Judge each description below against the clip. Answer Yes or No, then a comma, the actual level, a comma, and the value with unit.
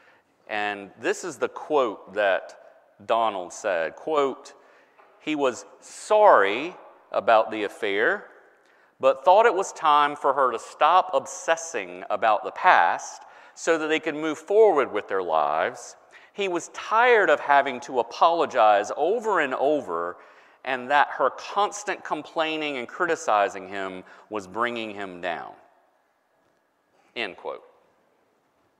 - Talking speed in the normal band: No, slow, 125 wpm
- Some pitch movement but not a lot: No, wide, 8.9 semitones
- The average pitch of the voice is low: No, medium, 155 Hz